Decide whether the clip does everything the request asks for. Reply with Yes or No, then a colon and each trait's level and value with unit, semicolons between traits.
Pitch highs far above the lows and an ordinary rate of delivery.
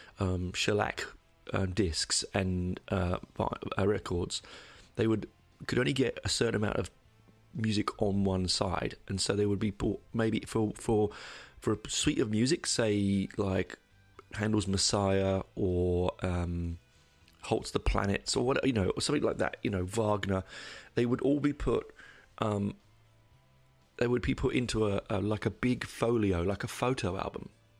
No: average, 2.7 semitones; average, 160 wpm